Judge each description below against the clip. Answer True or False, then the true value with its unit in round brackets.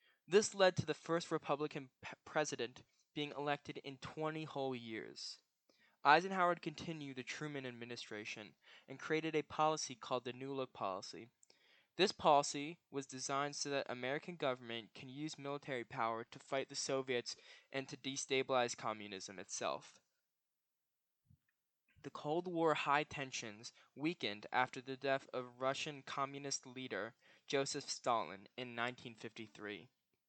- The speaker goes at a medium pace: False (130 wpm)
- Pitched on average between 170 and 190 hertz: False (135 Hz)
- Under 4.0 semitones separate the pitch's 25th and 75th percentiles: True (3.0 semitones)